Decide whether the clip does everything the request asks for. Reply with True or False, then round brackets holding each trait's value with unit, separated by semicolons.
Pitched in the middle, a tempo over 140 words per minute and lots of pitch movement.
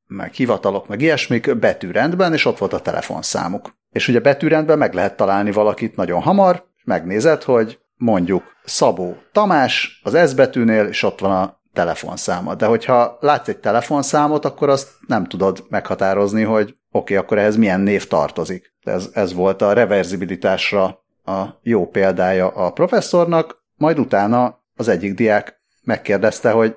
False (115 Hz; 150 wpm; 6.6 semitones)